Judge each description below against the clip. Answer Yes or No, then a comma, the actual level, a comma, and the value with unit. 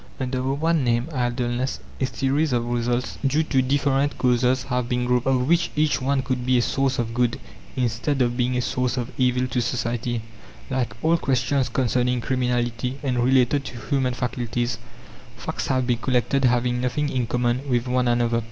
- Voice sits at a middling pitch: No, low, 125 Hz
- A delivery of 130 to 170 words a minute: No, average, 180 wpm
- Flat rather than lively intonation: Yes, narrow, 1.7 semitones